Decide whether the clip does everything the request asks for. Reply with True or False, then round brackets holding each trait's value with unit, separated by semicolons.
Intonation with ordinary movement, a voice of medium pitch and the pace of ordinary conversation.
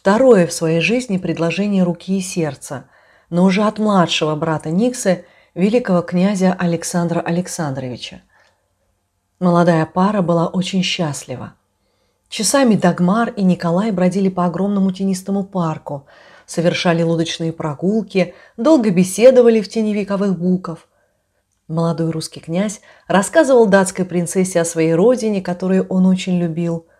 True (3.0 semitones; 180 Hz; 120 wpm)